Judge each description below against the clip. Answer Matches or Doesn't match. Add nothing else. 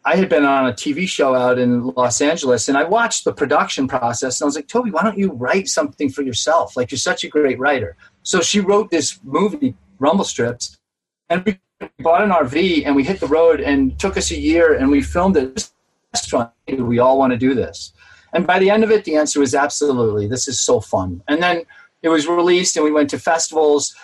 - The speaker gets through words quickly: Matches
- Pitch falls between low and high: Matches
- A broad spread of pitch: Matches